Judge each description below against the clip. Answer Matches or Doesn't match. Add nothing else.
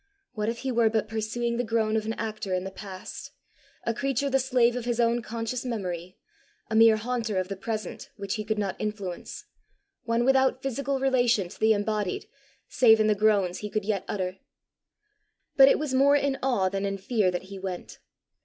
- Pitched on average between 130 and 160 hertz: Doesn't match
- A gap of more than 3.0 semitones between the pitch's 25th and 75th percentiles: Matches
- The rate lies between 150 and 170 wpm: Doesn't match